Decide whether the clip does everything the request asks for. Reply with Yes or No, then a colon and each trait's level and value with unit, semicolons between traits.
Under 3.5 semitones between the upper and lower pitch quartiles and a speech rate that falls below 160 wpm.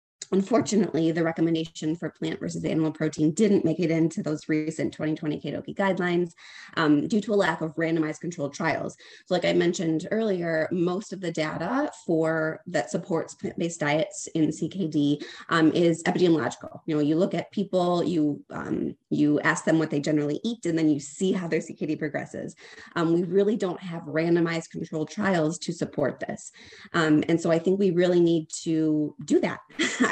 No: narrow, 2.5 semitones; average, 180 wpm